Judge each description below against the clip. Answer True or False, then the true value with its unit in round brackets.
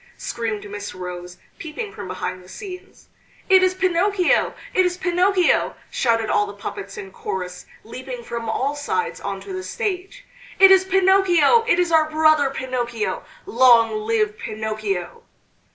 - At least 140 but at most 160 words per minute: True (150 wpm)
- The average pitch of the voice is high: True (275 Hz)